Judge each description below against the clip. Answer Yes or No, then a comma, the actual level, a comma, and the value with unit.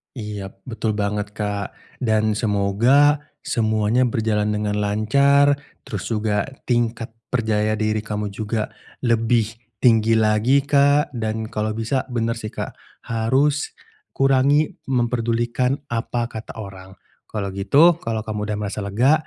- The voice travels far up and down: No, average, 2.8 semitones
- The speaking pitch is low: Yes, low, 110 Hz